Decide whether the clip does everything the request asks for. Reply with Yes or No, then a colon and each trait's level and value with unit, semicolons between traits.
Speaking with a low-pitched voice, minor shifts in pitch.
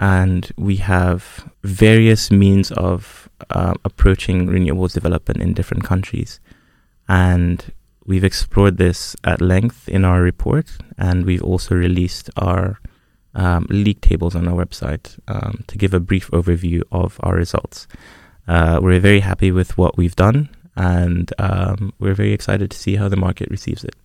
Yes: very low, 95 Hz; narrow, 2.1 semitones